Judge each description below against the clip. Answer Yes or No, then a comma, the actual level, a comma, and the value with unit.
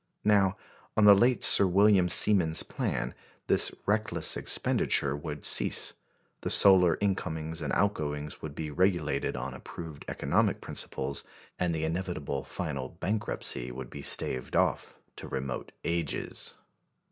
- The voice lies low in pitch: Yes, very low, 80 Hz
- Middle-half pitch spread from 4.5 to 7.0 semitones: Yes, average, 5.0 semitones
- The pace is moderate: No, slow, 130 wpm